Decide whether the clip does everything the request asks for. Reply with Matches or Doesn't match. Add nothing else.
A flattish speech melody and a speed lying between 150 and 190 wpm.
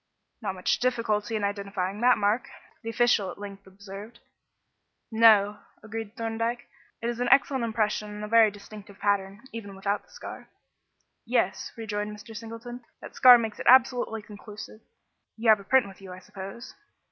Matches